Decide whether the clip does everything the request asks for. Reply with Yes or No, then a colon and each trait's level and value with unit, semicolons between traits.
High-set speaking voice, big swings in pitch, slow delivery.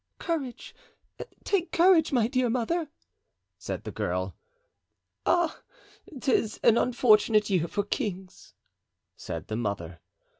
Yes: high, 235 Hz; wide, 7.2 semitones; slow, 110 wpm